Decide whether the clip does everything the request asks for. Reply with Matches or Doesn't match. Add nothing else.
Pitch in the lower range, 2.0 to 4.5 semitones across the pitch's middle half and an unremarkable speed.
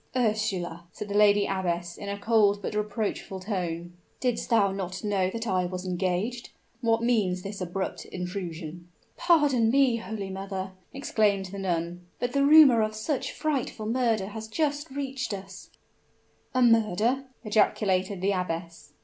Doesn't match